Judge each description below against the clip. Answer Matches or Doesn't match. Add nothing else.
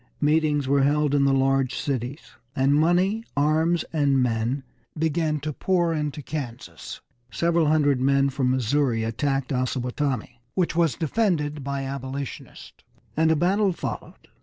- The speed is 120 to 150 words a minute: Matches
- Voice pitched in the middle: Matches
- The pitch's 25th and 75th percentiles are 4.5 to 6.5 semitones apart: Doesn't match